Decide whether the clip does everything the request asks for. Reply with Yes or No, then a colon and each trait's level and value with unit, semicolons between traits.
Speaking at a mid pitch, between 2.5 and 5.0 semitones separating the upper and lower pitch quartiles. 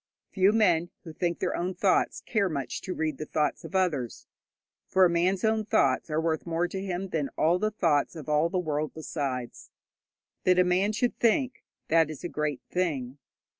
Yes: medium, 170 Hz; average, 3.5 semitones